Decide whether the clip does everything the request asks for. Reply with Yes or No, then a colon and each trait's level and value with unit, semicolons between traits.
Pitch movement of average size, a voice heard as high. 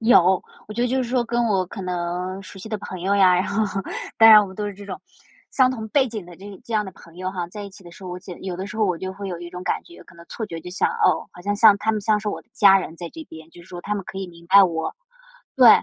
Yes: average, 3.1 semitones; high, 195 Hz